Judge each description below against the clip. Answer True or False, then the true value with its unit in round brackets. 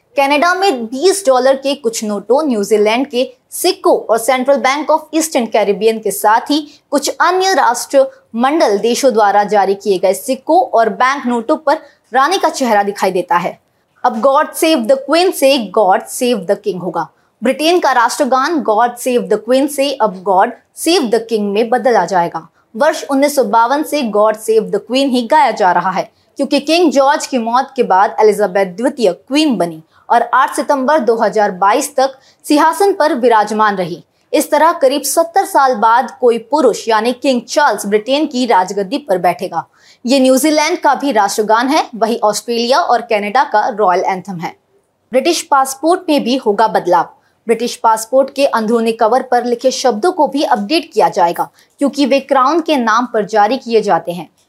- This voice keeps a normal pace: True (170 wpm)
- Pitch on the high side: True (255 Hz)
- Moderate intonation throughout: True (4.9 semitones)